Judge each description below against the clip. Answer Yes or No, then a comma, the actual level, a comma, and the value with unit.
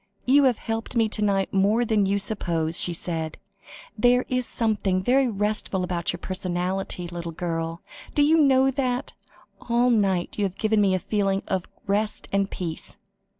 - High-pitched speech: Yes, high, 200 Hz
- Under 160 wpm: No, average, 170 wpm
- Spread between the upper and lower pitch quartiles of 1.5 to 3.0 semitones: No, average, 4.5 semitones